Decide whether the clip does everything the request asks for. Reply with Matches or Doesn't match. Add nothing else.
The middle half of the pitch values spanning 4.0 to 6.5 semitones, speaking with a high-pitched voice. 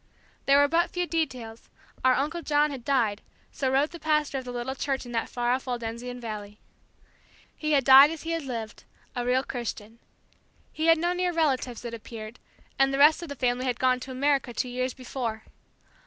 Doesn't match